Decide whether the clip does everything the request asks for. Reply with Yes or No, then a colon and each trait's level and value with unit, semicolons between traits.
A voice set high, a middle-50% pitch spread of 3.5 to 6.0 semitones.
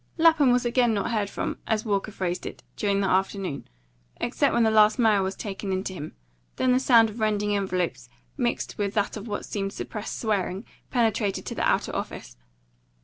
No: high, 210 Hz; average, 3.0 semitones